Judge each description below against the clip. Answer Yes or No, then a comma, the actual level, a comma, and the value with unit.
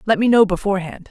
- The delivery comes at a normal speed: No, fast, 220 wpm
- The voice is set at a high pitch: Yes, high, 200 Hz